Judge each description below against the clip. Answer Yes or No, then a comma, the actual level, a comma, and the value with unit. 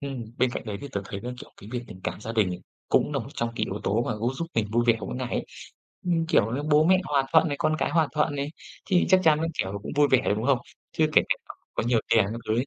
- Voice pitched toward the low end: Yes, low, 125 Hz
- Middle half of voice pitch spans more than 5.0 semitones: Yes, wide, 5.4 semitones